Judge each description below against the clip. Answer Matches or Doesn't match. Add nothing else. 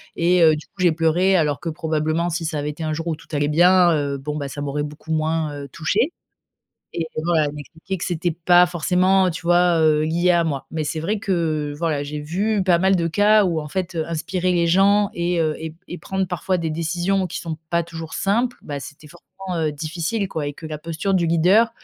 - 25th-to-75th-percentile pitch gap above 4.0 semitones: Doesn't match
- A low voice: Doesn't match